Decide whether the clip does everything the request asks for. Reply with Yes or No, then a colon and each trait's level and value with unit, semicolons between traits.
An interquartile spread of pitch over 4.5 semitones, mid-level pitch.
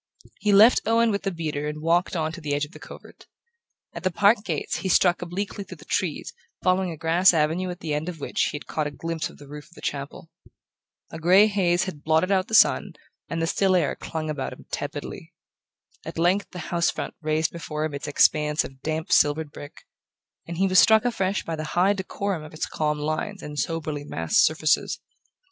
No: average, 3.5 semitones; medium, 165 Hz